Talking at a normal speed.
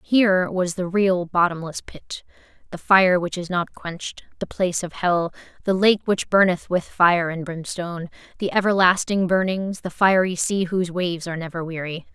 Yes: average, 175 wpm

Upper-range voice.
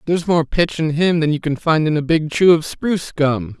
No: medium, 160 Hz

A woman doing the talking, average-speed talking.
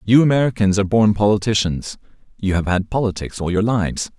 No: male; average, 170 wpm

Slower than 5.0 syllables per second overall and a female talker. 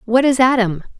No: 5.3 syllables/s; female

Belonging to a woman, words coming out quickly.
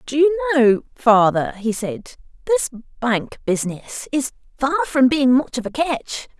No: female; average, 160 wpm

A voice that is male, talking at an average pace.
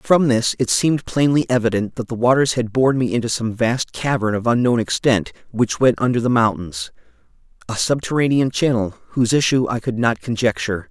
Yes: male; average, 175 wpm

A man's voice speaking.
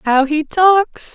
No: female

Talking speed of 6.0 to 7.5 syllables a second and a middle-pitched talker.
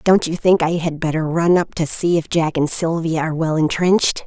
No: 5.3 syllables/s; medium, 165 Hz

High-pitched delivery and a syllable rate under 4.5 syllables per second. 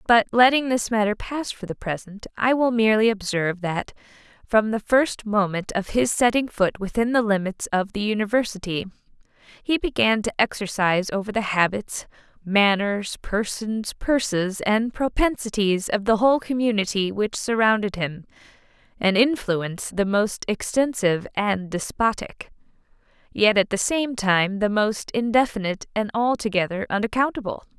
No: high, 215 Hz; 4.9 syllables/s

